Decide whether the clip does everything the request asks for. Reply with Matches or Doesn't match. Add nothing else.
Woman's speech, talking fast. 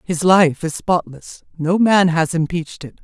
Doesn't match